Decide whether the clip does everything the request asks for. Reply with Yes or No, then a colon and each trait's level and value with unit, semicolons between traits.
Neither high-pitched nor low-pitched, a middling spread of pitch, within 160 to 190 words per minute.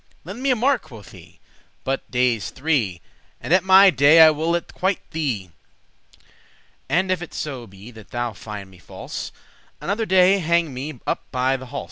No: medium, 150 Hz; wide, 7.1 semitones; average, 180 wpm